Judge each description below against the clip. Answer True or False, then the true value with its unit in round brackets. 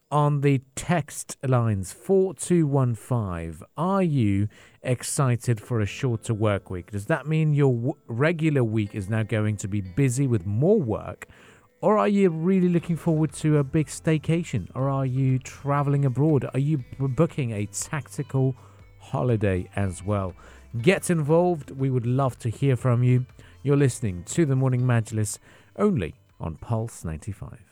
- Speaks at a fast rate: False (155 wpm)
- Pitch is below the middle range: True (130 Hz)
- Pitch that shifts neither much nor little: False (5.9 semitones)